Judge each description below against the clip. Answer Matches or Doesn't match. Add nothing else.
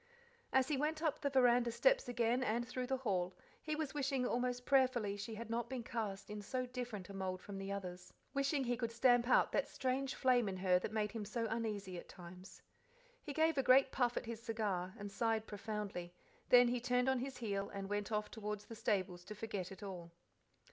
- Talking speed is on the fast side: Matches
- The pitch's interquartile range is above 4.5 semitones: Doesn't match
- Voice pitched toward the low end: Doesn't match